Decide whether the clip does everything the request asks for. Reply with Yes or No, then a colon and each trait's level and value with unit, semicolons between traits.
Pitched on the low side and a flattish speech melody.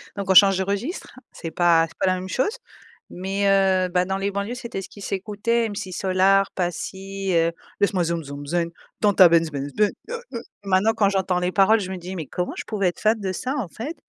No: high, 190 Hz; narrow, 2.2 semitones